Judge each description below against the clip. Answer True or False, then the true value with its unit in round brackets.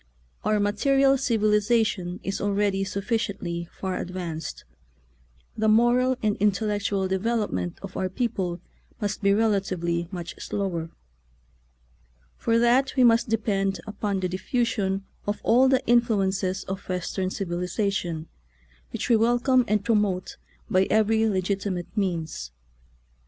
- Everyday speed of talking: False (125 wpm)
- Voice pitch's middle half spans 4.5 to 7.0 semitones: False (3.3 semitones)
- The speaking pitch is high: True (200 Hz)